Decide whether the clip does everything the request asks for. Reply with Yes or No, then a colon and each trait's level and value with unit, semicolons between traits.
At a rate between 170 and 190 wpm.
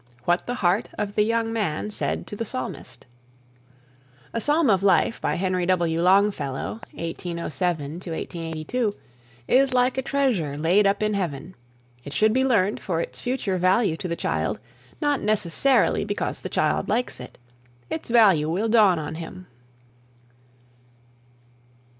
No: average, 145 wpm